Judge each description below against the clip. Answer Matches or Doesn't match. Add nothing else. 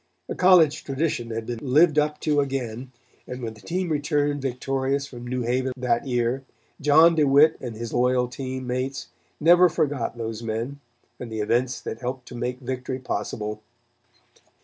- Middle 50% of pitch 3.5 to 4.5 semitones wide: Doesn't match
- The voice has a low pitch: Matches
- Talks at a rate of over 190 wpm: Doesn't match